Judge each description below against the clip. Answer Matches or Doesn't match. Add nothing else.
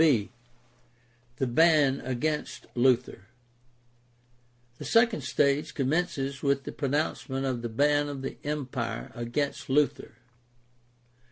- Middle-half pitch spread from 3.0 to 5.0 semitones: Matches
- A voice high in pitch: Doesn't match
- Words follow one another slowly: Matches